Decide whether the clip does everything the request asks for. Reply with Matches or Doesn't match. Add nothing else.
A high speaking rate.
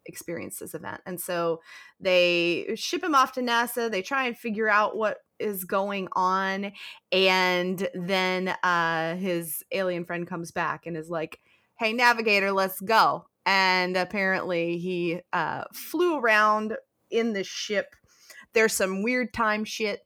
Doesn't match